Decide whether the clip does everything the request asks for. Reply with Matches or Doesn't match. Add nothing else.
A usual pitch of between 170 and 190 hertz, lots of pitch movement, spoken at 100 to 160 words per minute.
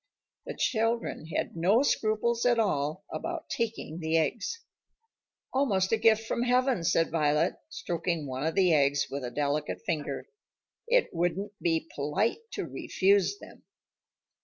Matches